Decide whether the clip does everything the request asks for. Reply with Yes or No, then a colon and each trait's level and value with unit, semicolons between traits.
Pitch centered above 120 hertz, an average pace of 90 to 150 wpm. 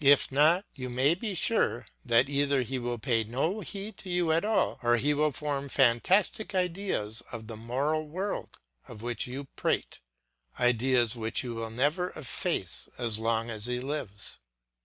No: low, 135 Hz; average, 170 wpm